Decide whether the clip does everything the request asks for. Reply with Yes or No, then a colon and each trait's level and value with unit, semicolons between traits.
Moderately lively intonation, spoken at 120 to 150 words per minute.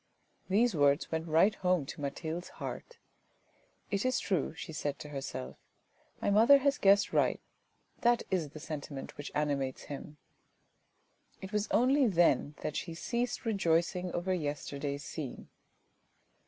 No: wide, 6.2 semitones; average, 145 wpm